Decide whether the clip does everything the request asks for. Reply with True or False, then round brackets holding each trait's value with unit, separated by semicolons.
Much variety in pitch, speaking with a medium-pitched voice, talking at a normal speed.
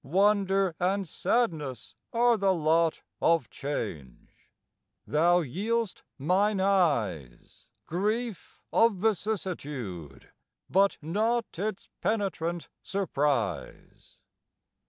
False (5.8 semitones; 180 Hz; 80 wpm)